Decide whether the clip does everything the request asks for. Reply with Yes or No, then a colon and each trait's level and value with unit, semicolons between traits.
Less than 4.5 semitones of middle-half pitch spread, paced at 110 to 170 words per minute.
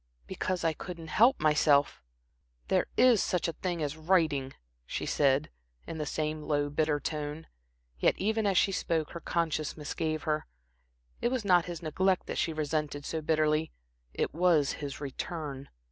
Yes: average, 2.8 semitones; average, 160 wpm